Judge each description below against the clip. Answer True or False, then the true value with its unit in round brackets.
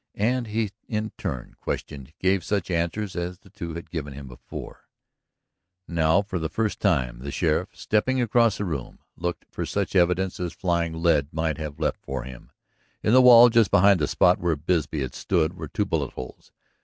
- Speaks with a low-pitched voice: True (85 Hz)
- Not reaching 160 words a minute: False (190 wpm)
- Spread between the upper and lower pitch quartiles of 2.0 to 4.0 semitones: False (4.7 semitones)